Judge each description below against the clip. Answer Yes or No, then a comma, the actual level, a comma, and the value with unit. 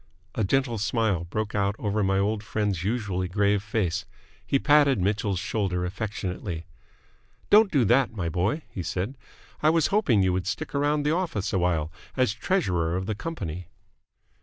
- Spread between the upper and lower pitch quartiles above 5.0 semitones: Yes, wide, 5.6 semitones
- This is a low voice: Yes, low, 105 Hz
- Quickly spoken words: No, average, 160 wpm